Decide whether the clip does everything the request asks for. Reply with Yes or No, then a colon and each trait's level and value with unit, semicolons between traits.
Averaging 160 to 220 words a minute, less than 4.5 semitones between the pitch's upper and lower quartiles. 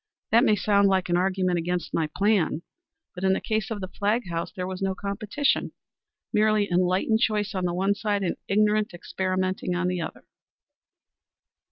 Yes: average, 175 wpm; narrow, 2.6 semitones